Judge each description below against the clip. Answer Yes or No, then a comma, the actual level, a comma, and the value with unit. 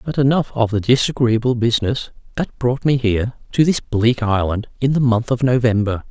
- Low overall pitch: Yes, low, 120 Hz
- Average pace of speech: Yes, average, 185 wpm